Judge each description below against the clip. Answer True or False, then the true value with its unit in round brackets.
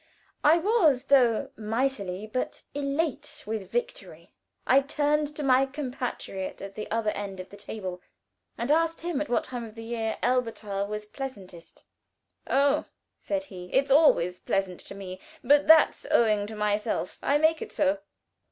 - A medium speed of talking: True (160 wpm)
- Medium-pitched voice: False (245 Hz)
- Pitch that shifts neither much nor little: False (5.7 semitones)